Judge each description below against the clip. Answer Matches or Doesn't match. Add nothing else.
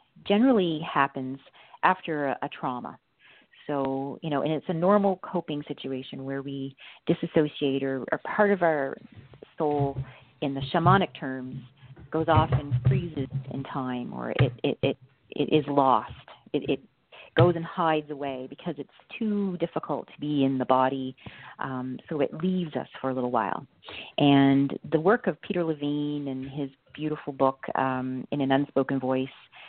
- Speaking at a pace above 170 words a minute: Doesn't match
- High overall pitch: Doesn't match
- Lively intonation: Doesn't match